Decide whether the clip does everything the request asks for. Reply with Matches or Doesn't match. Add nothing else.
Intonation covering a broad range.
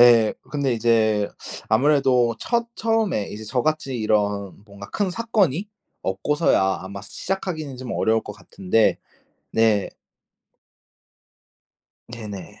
Matches